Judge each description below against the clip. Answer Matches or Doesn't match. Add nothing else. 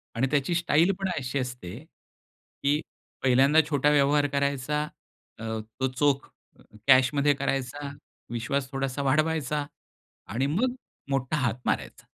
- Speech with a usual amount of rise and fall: Doesn't match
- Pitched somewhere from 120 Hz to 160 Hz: Matches